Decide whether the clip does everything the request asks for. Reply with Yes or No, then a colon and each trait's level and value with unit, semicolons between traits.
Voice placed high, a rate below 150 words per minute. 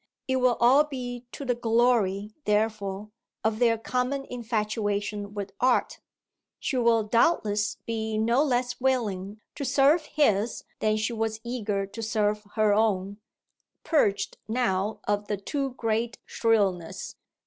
Yes: high, 220 Hz; slow, 135 wpm